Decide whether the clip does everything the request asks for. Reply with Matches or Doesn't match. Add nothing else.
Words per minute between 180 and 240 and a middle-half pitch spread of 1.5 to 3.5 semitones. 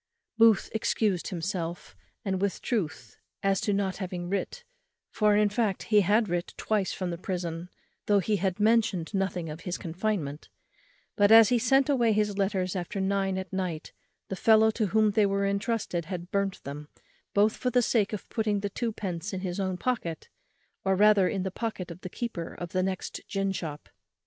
Matches